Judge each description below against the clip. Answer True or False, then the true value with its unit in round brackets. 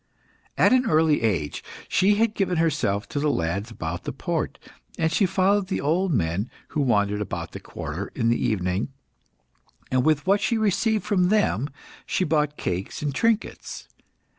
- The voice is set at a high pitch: False (150 Hz)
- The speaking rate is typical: True (165 wpm)